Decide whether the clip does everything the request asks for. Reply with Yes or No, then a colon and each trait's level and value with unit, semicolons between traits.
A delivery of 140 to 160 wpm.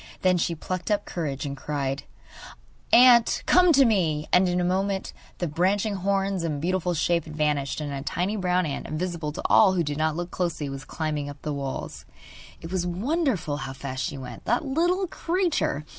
No: average, 190 wpm